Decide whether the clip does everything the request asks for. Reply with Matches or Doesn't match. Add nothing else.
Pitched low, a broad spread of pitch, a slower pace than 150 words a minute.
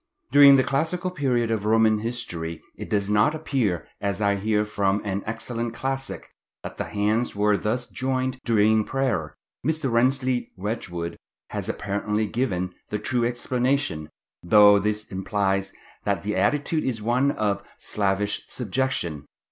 Doesn't match